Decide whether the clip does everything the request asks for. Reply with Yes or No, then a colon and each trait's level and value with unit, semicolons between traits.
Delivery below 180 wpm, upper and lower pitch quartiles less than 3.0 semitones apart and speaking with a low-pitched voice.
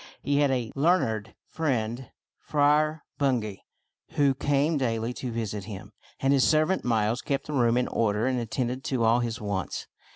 No: average, 165 wpm; average, 4.0 semitones; low, 125 Hz